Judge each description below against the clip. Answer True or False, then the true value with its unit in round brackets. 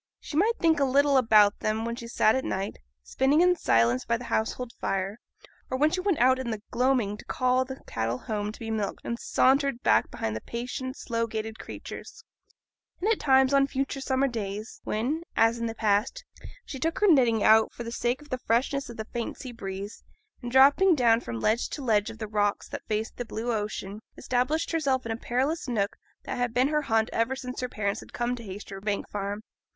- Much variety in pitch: False (3.6 semitones)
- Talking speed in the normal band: False (215 wpm)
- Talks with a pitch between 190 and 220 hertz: False (235 Hz)